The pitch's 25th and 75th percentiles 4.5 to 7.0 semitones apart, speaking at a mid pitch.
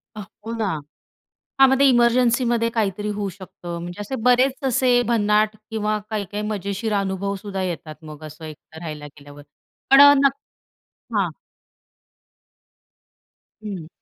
No: average, 4.8 semitones; high, 205 Hz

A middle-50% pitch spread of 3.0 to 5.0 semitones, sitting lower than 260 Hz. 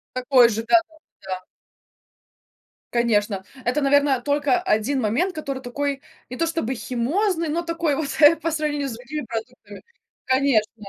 No: average, 4.3 semitones; very high, 275 Hz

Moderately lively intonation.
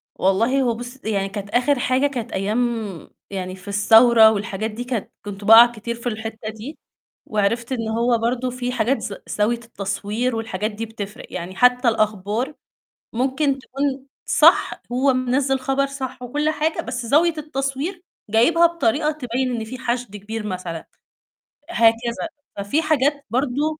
Yes: average, 3.7 semitones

